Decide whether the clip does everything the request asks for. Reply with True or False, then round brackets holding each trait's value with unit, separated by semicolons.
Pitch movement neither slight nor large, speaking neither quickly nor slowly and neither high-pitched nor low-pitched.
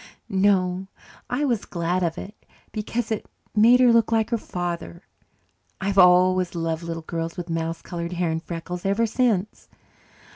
True (4.2 semitones; 155 wpm; 180 Hz)